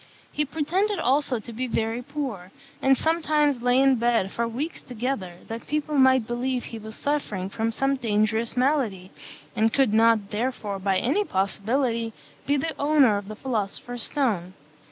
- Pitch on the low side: No, high, 240 Hz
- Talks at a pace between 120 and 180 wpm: Yes, average, 160 wpm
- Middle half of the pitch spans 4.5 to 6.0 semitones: No, average, 4.1 semitones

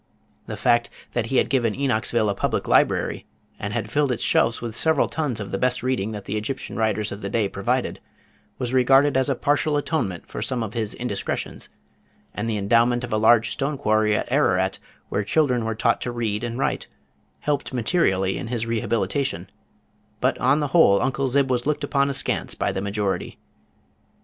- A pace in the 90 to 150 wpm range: No, average, 190 wpm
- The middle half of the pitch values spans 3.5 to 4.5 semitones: Yes, average, 3.9 semitones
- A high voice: No, low, 120 Hz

